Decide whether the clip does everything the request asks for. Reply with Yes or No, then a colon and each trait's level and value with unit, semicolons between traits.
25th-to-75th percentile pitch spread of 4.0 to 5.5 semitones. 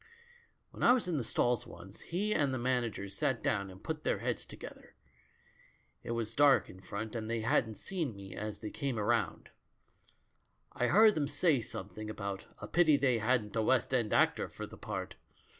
Yes: average, 5.2 semitones